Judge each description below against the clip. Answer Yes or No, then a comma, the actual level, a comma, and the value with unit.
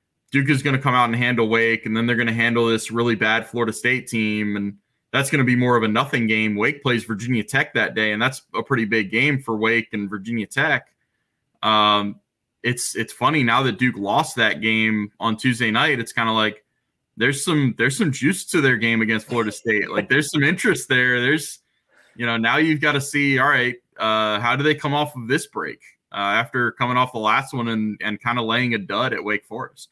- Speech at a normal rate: No, fast, 235 wpm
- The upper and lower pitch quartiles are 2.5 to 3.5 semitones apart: Yes, average, 2.8 semitones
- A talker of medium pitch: No, low, 115 Hz